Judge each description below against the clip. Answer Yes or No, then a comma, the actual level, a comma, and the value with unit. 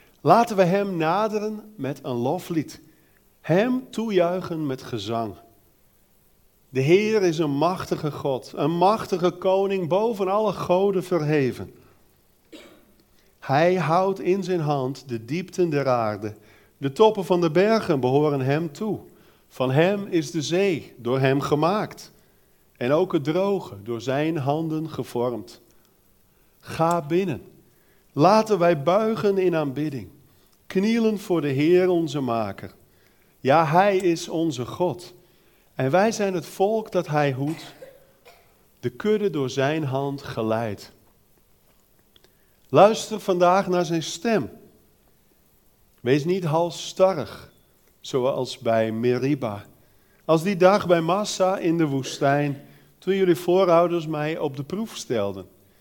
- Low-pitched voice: No, medium, 165 Hz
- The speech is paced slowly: Yes, slow, 125 wpm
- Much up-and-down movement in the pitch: Yes, wide, 5.8 semitones